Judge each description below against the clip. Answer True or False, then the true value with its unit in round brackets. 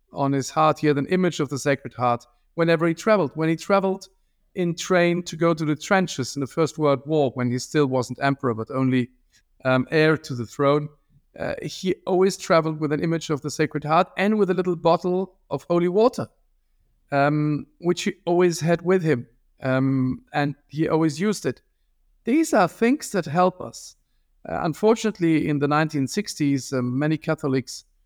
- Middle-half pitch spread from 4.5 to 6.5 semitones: True (4.8 semitones)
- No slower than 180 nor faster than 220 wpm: True (185 wpm)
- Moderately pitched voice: True (155 Hz)